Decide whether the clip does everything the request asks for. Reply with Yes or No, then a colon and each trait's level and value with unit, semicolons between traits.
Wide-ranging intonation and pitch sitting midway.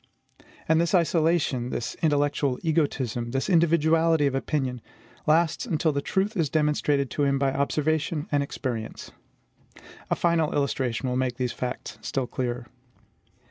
No: average, 3.7 semitones; medium, 145 Hz